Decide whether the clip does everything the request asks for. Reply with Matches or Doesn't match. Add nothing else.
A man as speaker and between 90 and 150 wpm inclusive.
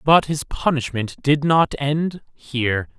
Matches